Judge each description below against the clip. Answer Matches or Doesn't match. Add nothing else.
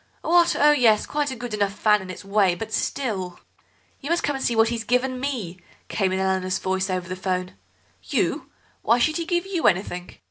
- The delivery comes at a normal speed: Doesn't match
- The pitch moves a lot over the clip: Matches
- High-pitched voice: Matches